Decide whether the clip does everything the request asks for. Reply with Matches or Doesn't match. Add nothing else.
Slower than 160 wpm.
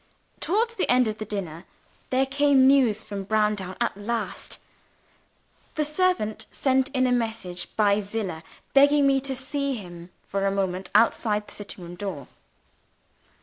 Matches